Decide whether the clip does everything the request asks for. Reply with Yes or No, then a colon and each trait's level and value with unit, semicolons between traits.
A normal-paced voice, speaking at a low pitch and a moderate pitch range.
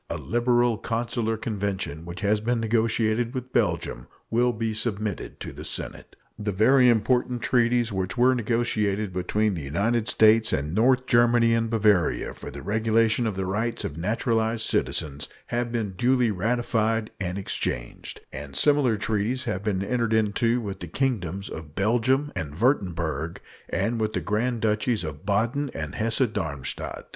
Yes: average, 155 wpm; low, 110 Hz; average, 3.4 semitones